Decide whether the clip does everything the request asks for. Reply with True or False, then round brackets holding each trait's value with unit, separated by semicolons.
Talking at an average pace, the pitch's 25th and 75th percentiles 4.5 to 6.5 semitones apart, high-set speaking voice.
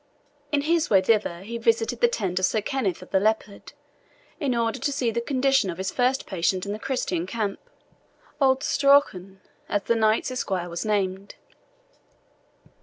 True (170 wpm; 4.9 semitones; 220 Hz)